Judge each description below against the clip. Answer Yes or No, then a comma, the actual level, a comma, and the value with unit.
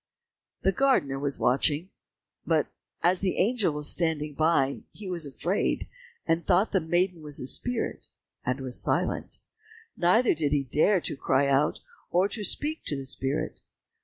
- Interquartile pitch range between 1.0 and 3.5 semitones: No, average, 5.1 semitones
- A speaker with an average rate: Yes, average, 160 wpm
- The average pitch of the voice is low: No, medium, 160 Hz